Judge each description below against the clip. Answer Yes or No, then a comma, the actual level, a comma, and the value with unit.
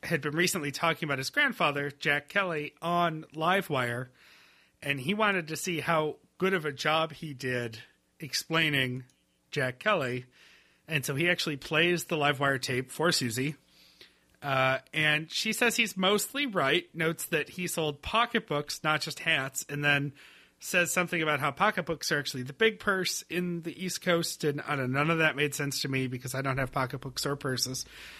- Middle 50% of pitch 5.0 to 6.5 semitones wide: No, average, 4.2 semitones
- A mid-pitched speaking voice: Yes, medium, 150 Hz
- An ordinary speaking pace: Yes, average, 185 wpm